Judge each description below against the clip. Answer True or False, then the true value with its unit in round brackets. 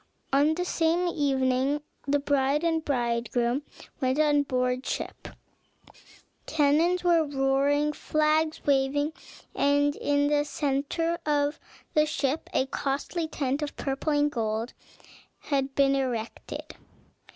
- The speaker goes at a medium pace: False (120 wpm)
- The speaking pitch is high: True (285 Hz)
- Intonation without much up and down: True (2.2 semitones)